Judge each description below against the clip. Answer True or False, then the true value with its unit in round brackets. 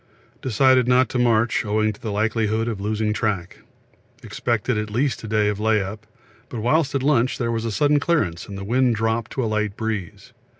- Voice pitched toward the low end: True (110 Hz)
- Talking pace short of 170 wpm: False (195 wpm)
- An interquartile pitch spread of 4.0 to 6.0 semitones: False (2.7 semitones)